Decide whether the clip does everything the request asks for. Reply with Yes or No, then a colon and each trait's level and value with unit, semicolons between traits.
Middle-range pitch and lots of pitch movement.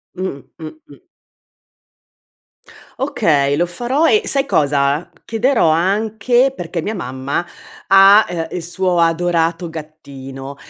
Yes: medium, 175 Hz; wide, 6.0 semitones